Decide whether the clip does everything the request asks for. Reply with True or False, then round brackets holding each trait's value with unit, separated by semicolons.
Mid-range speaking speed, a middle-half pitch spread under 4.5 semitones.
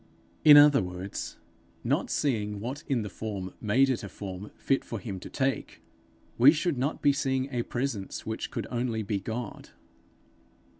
False (165 wpm; 4.8 semitones)